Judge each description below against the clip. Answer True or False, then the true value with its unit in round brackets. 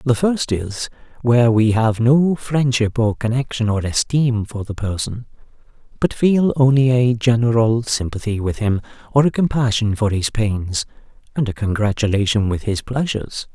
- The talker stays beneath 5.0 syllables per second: True (4.7 syllables/s)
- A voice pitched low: True (115 Hz)